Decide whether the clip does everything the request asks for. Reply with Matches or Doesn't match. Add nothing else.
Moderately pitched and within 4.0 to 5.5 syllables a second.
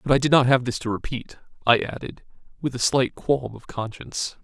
Doesn't match